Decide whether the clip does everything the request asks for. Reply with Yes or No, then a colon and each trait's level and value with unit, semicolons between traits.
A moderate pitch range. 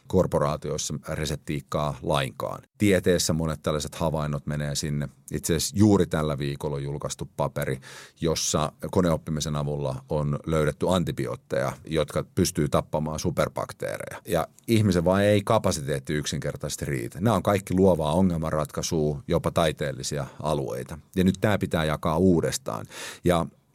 Yes: average, 4.1 semitones